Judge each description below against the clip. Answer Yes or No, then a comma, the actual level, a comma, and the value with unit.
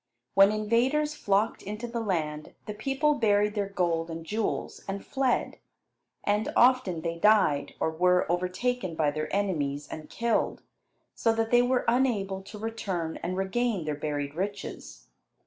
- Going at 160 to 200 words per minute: No, average, 150 wpm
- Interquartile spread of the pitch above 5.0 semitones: Yes, wide, 5.5 semitones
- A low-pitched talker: No, high, 200 Hz